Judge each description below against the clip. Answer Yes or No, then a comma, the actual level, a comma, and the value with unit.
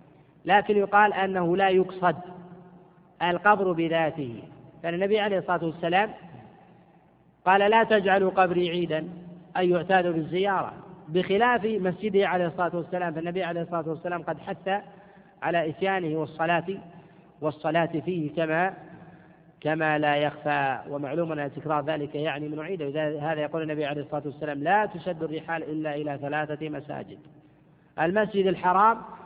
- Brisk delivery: No, average, 125 wpm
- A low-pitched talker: No, medium, 170 Hz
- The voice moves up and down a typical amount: Yes, average, 3.1 semitones